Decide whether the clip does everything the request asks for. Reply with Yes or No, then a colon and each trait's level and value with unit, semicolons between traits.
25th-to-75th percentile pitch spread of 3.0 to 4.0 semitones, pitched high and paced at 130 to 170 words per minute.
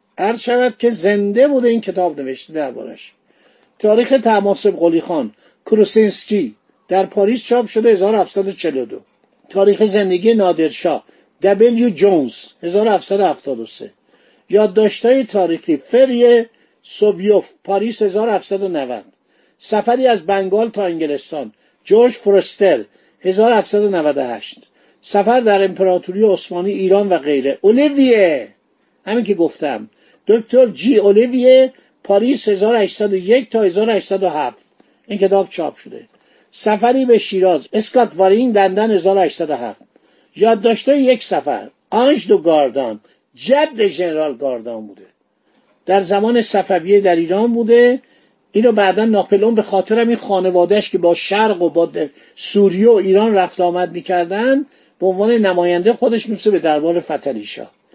No: average, 3.7 semitones; high, 205 Hz; average, 115 wpm